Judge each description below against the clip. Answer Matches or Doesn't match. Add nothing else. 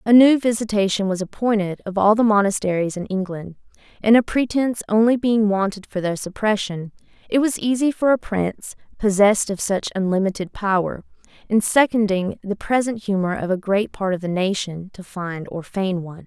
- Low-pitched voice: Doesn't match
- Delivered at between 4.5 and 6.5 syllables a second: Matches